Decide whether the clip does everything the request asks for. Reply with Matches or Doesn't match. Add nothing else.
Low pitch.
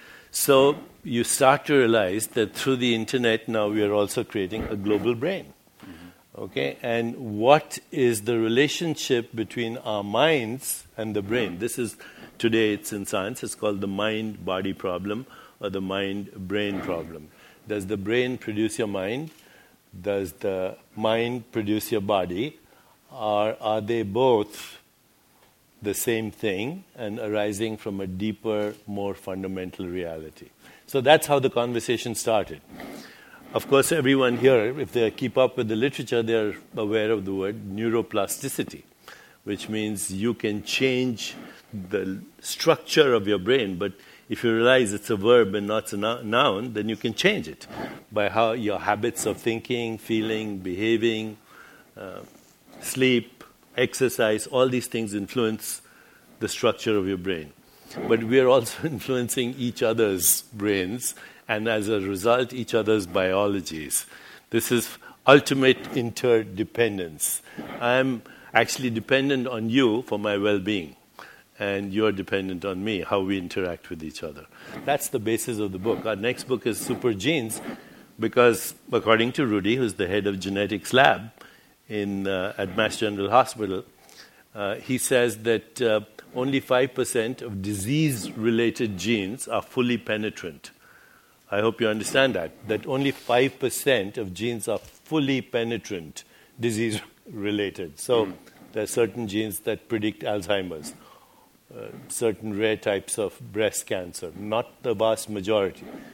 Matches